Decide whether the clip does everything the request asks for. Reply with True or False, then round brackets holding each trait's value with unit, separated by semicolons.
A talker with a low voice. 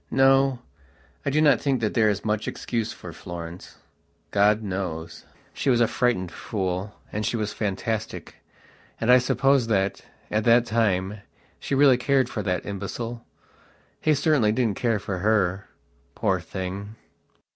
True (110 Hz)